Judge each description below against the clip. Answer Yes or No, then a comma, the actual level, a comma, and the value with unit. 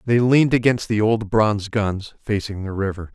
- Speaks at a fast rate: No, average, 190 wpm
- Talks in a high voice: No, low, 110 Hz